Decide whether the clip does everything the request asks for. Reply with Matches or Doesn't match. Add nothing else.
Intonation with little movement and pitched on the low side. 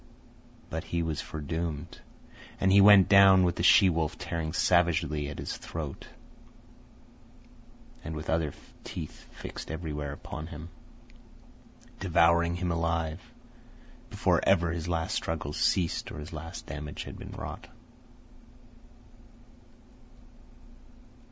Matches